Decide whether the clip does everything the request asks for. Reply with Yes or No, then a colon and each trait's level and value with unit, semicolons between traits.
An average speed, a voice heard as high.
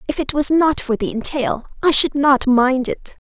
No: fast, 220 wpm; very high, 270 Hz